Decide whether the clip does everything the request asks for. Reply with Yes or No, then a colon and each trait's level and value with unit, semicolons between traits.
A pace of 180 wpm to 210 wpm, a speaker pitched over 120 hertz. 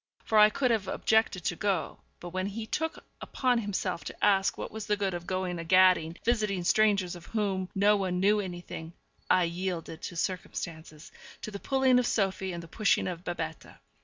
Yes: average, 190 wpm; high, 190 Hz